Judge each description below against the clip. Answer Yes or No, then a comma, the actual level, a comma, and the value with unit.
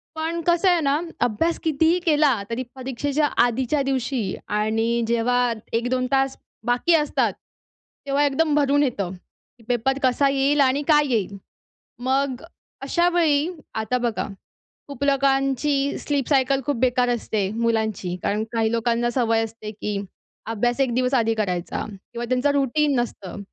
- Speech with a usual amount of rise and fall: Yes, average, 3.7 semitones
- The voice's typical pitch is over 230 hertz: Yes, very high, 255 Hz